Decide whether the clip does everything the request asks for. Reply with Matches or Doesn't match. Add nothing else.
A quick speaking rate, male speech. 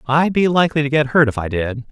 Matches